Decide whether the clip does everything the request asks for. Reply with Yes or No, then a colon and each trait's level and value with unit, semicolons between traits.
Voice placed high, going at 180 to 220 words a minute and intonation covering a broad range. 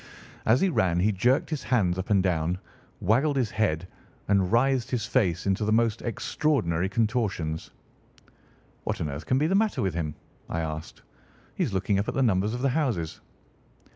No: low, 105 Hz; average, 185 wpm; wide, 5.9 semitones